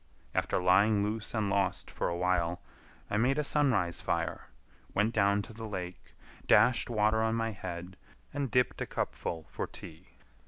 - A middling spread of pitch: Yes, average, 3.6 semitones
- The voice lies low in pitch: Yes, low, 105 Hz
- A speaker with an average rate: Yes, average, 160 wpm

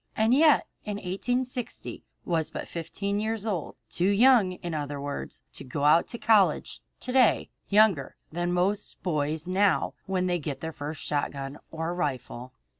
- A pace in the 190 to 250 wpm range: No, average, 160 wpm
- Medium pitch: Yes, medium, 180 Hz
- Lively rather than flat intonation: Yes, wide, 5.7 semitones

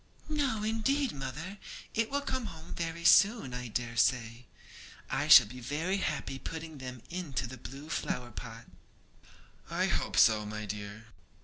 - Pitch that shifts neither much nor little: No, wide, 8.4 semitones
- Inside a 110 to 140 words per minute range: No, average, 150 wpm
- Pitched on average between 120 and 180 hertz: Yes, low, 135 Hz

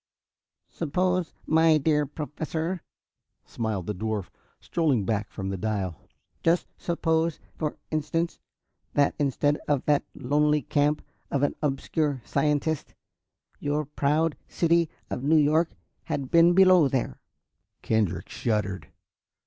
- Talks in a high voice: No, medium, 150 Hz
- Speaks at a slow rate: Yes, slow, 115 wpm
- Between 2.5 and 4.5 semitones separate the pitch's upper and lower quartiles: Yes, average, 4.2 semitones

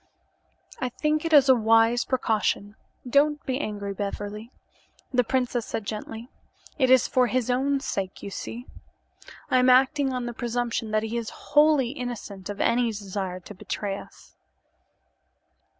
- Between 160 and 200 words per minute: No, average, 150 wpm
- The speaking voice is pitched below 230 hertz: No, high, 240 Hz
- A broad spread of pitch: No, average, 3.4 semitones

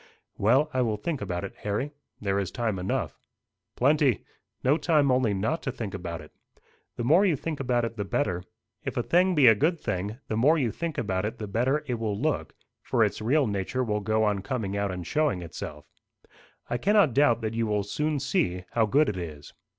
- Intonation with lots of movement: Yes, wide, 6.2 semitones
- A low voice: Yes, low, 115 Hz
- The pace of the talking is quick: Yes, fast, 215 wpm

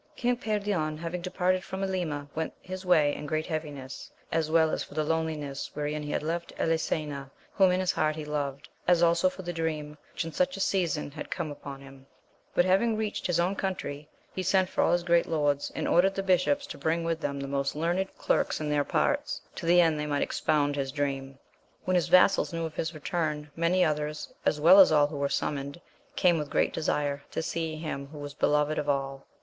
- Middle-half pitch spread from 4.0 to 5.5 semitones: No, average, 3.4 semitones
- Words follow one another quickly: Yes, fast, 210 wpm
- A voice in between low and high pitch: Yes, medium, 160 Hz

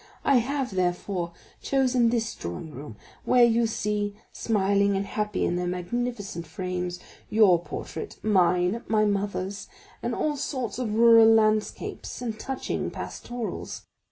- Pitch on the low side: No, high, 210 Hz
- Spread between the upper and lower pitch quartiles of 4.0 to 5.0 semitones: Yes, average, 4.3 semitones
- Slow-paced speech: Yes, slow, 130 wpm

